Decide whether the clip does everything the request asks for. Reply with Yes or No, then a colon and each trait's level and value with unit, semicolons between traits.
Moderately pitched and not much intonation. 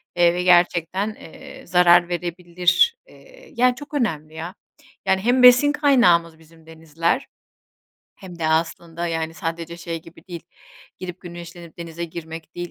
Yes: medium, 175 Hz; narrow, 2.1 semitones